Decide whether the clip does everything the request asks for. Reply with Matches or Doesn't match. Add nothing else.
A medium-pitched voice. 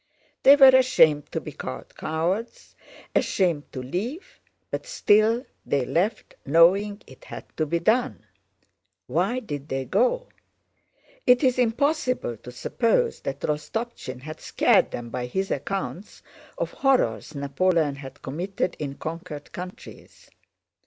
Matches